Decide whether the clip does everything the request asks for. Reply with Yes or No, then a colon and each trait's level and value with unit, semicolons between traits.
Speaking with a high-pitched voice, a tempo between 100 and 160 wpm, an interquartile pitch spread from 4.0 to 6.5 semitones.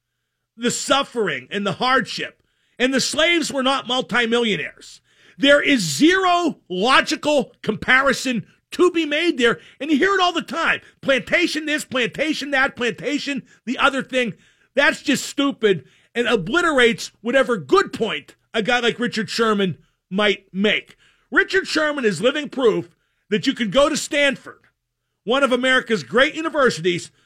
Yes: very high, 255 Hz; average, 145 wpm; average, 4.9 semitones